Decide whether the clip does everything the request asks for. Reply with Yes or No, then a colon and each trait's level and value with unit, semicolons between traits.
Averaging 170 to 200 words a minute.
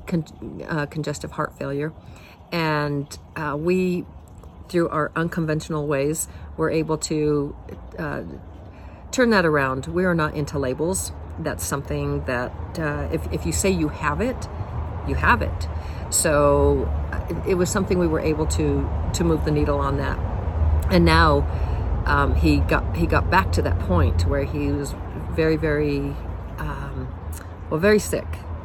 No: average, 155 wpm